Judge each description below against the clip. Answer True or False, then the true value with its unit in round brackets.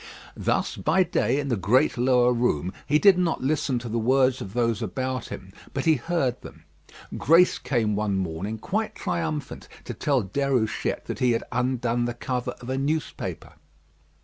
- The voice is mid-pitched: False (125 Hz)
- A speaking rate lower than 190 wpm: True (175 wpm)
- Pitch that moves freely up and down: False (3.6 semitones)